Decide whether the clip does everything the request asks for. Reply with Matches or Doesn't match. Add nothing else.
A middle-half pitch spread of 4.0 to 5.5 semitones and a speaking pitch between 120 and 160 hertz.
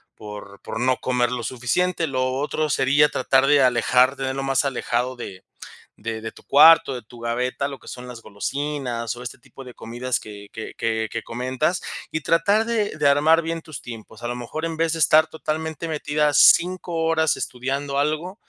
Matches